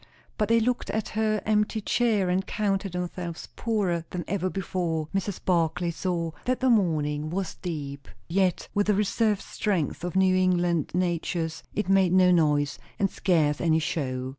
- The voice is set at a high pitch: No, medium, 180 Hz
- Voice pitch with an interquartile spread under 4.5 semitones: Yes, average, 3.6 semitones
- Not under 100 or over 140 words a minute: No, average, 165 wpm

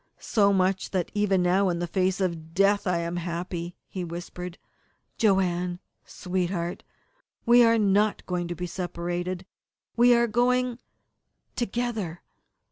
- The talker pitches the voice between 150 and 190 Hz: Yes, medium, 185 Hz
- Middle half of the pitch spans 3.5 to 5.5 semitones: No, average, 2.9 semitones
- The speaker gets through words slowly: Yes, slow, 130 wpm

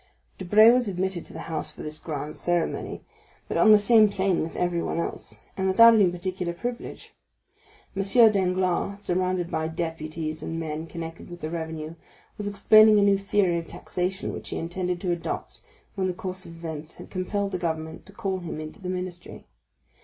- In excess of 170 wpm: Yes, average, 185 wpm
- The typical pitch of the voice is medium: Yes, medium, 180 Hz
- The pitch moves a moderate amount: Yes, average, 3.1 semitones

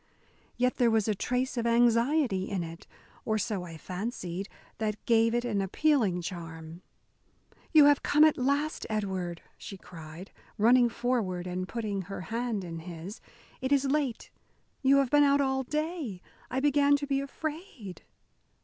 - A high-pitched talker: Yes, high, 230 Hz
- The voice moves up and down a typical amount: No, wide, 6.6 semitones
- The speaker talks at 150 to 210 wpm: Yes, average, 160 wpm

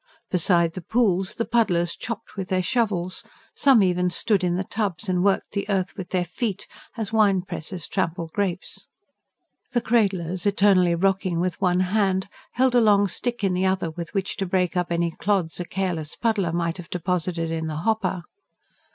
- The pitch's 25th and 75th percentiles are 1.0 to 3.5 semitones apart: Yes, narrow, 2.6 semitones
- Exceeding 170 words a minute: Yes, average, 180 wpm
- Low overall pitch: No, medium, 185 Hz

